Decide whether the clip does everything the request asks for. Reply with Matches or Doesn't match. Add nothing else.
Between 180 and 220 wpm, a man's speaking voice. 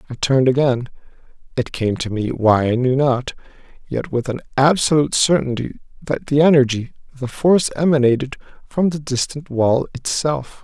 Doesn't match